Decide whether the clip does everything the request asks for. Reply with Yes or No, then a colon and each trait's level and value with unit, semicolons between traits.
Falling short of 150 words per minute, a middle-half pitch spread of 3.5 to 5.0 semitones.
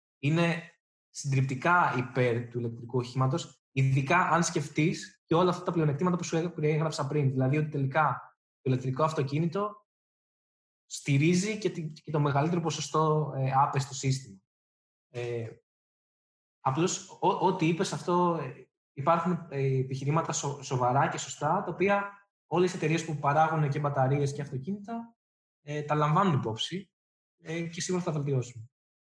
Yes: average, 130 wpm; average, 4.2 semitones